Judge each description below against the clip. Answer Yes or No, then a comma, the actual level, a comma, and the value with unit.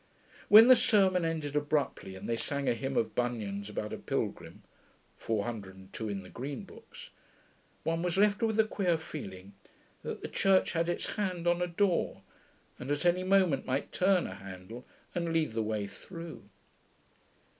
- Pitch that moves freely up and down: Yes, wide, 8.4 semitones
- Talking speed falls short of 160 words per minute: No, average, 165 wpm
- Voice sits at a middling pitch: Yes, medium, 150 Hz